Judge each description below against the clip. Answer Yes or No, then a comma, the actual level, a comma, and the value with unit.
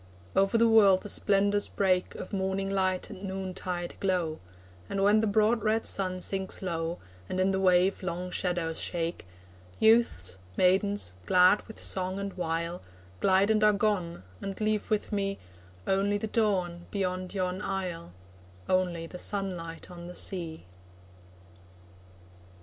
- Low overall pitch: No, high, 190 Hz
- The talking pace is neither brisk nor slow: Yes, average, 145 wpm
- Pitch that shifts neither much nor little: No, narrow, 2.1 semitones